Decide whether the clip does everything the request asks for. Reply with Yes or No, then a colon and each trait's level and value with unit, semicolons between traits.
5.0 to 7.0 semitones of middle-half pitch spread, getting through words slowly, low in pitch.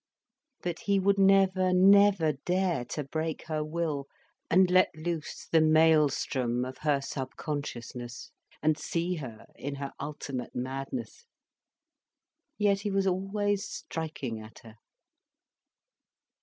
No: average, 5.3 semitones; slow, 115 wpm; medium, 160 Hz